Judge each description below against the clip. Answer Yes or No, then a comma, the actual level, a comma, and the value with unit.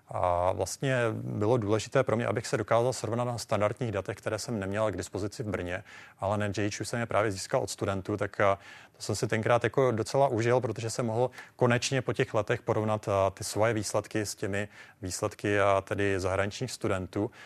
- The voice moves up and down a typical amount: Yes, average, 3.0 semitones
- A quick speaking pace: Yes, fast, 180 wpm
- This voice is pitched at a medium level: No, low, 110 Hz